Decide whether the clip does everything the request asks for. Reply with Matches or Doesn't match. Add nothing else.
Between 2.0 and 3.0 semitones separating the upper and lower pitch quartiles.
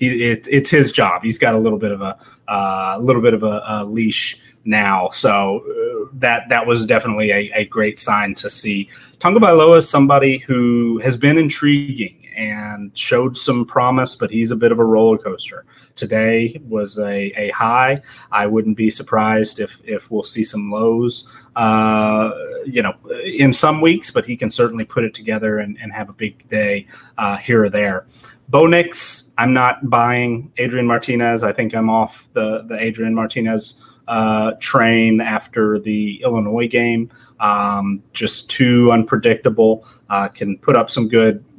Matches